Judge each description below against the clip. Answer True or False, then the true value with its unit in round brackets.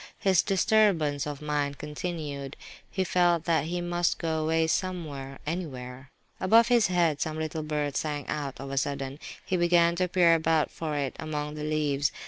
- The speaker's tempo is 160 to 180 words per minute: True (170 wpm)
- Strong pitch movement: False (3.2 semitones)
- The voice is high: False (155 Hz)